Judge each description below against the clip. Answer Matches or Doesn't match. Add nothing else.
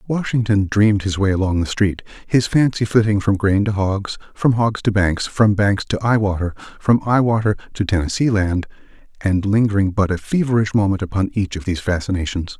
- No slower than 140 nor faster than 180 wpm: Doesn't match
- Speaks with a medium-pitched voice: Doesn't match